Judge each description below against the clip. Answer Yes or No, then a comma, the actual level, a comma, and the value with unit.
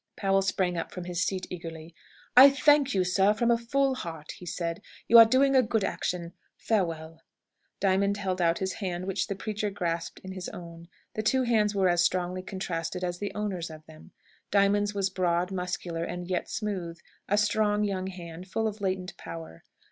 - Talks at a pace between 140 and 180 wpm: No, average, 190 wpm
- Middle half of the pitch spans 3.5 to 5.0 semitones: No, average, 3.1 semitones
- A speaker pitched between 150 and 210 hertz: Yes, medium, 185 Hz